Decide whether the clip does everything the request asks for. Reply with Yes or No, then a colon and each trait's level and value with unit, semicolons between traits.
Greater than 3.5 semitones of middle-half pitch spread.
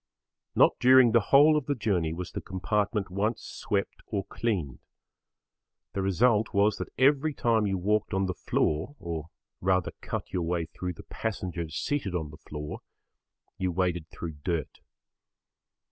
Yes: average, 4.6 semitones